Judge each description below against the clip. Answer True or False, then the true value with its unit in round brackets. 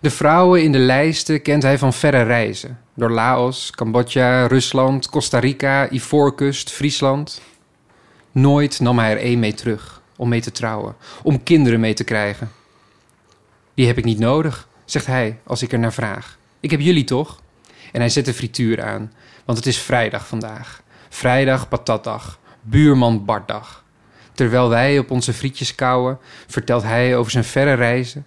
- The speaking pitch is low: True (125 Hz)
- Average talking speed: True (165 wpm)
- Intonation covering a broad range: False (2.8 semitones)